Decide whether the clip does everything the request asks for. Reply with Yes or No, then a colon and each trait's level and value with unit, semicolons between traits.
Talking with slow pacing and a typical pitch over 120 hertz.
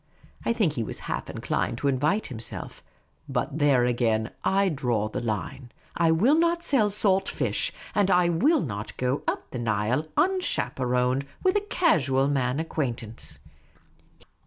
No: average, 155 wpm; medium, 140 Hz